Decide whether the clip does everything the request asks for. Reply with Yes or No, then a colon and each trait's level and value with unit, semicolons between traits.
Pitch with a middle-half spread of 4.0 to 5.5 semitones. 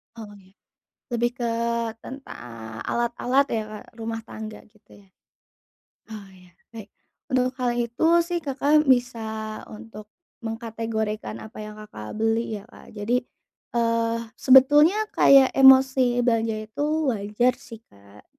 No: average, 2.8 semitones